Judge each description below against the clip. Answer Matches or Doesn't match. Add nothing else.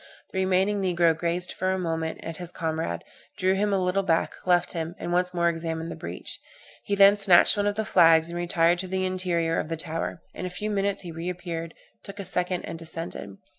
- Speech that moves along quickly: Matches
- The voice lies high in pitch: Doesn't match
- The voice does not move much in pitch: Matches